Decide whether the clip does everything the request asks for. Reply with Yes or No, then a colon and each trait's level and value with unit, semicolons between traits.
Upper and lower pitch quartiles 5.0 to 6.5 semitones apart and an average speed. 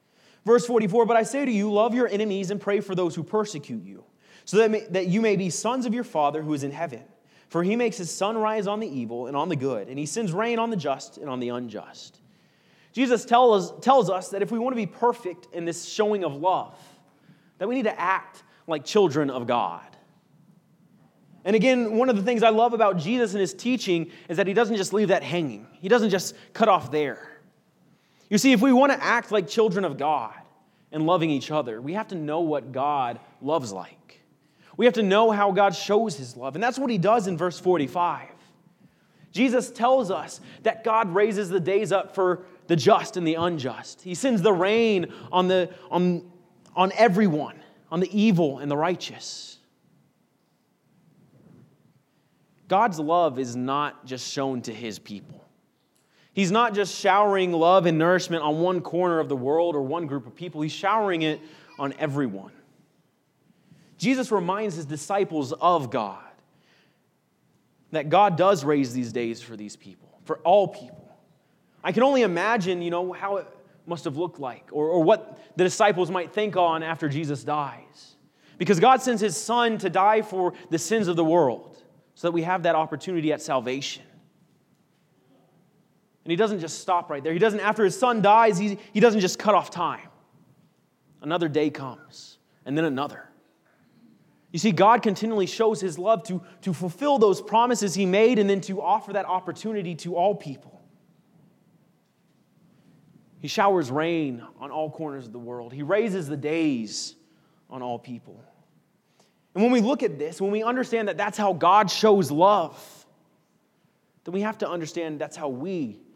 Yes: average, 5.3 semitones; average, 185 wpm